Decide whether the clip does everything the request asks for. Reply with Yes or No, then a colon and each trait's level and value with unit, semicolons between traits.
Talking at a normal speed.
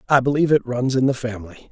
No: fast, 245 wpm